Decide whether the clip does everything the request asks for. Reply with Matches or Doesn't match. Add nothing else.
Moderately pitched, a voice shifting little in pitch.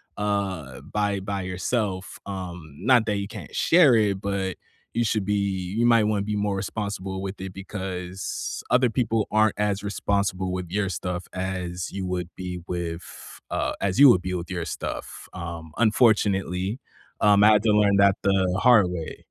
Doesn't match